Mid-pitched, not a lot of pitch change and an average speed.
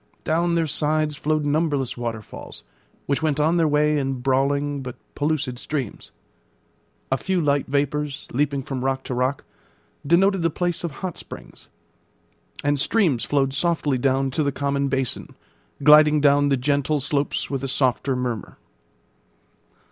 Yes: medium, 145 Hz; narrow, 2.3 semitones; average, 150 wpm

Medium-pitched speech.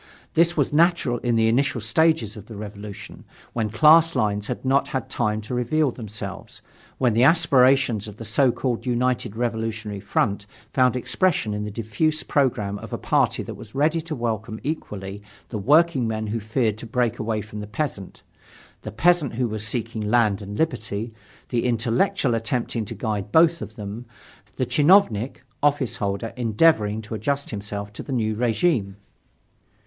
No: low, 115 Hz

